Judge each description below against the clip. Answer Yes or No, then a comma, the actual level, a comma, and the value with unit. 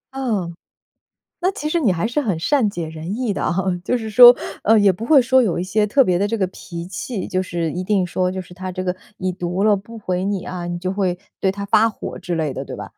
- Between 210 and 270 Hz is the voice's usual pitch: No, high, 190 Hz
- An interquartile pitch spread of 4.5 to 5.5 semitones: No, average, 3.8 semitones